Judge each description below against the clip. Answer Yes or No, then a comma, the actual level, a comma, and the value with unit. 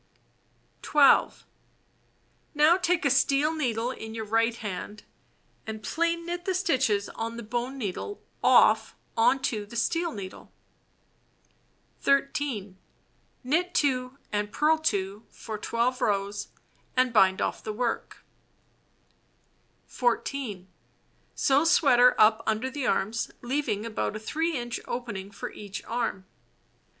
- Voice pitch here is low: No, high, 240 Hz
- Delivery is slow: Yes, slow, 120 wpm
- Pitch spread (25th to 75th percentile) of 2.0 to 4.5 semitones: No, average, 5.0 semitones